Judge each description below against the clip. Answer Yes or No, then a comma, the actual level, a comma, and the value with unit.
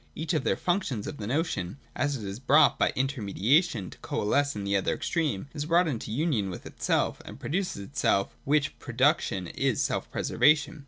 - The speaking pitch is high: No, low, 135 Hz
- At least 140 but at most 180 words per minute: No, average, 190 wpm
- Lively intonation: Yes, wide, 7.2 semitones